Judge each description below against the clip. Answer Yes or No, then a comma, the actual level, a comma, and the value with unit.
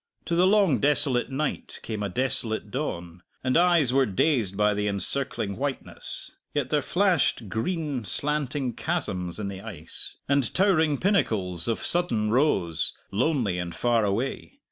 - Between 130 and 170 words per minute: Yes, average, 145 wpm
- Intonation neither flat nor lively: No, wide, 6.9 semitones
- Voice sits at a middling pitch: No, low, 125 Hz